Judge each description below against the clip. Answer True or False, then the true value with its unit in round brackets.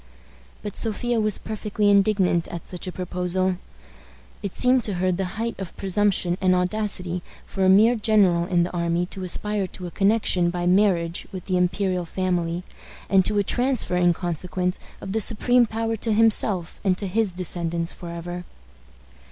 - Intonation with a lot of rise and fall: False (3.0 semitones)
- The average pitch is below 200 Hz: True (185 Hz)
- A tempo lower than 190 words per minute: True (170 wpm)